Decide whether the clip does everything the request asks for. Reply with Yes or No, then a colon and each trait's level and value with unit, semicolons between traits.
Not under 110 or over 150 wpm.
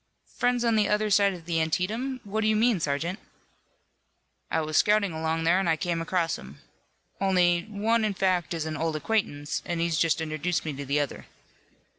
No: average, 195 wpm